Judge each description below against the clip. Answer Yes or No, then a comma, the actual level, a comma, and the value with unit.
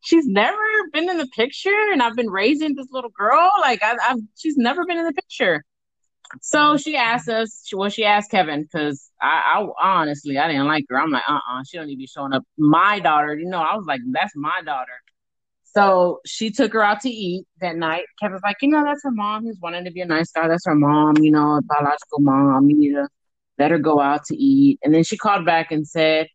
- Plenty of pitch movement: Yes, wide, 9.0 semitones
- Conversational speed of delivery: No, fast, 240 wpm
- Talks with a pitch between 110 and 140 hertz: No, high, 195 Hz